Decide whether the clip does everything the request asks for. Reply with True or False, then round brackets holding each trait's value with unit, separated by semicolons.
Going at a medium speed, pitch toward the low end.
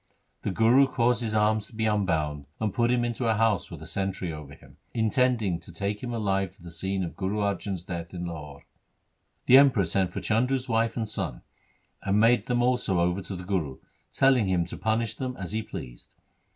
False (210 wpm; 105 Hz)